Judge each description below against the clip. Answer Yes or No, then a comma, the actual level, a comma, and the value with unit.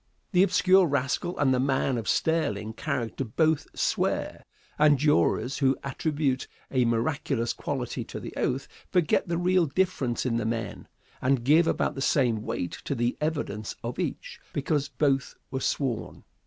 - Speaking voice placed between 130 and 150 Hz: Yes, low, 135 Hz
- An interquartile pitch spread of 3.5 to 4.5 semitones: Yes, average, 4.2 semitones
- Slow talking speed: No, average, 155 wpm